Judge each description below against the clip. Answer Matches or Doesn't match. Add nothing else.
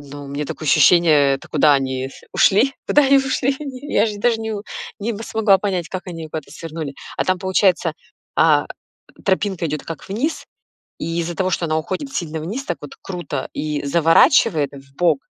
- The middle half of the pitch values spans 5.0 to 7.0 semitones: Matches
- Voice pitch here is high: Doesn't match